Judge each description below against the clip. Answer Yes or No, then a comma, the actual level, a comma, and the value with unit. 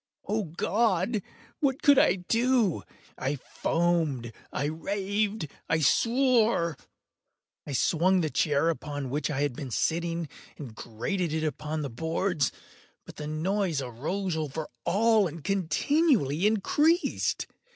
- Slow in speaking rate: Yes, slow, 120 wpm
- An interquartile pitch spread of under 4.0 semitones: No, wide, 5.4 semitones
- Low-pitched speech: No, medium, 170 Hz